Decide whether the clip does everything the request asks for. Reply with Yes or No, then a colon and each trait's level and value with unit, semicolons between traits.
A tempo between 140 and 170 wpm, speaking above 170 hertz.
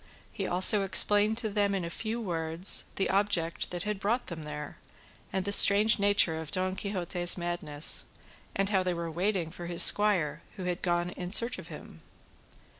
No: average, 185 wpm; medium, 185 Hz